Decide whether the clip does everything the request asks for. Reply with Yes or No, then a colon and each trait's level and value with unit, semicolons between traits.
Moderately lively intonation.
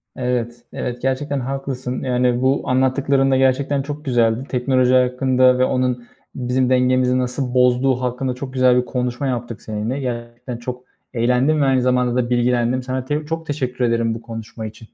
No: narrow, 1.3 semitones